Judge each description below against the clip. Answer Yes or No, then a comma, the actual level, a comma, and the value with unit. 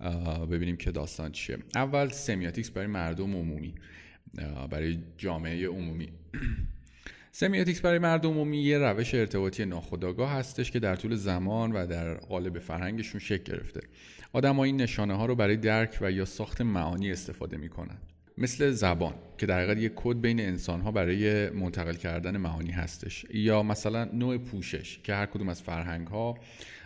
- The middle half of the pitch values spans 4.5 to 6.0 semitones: Yes, average, 5.1 semitones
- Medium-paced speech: No, fast, 160 wpm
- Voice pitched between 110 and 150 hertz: No, very low, 95 Hz